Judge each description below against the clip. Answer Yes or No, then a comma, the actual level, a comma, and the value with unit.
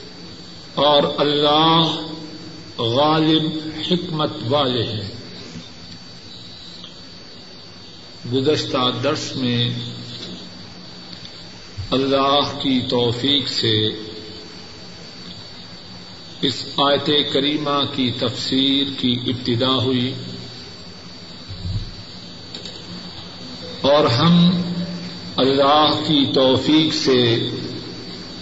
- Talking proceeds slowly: Yes, slow, 55 wpm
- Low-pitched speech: Yes, low, 130 Hz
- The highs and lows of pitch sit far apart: Yes, wide, 8.7 semitones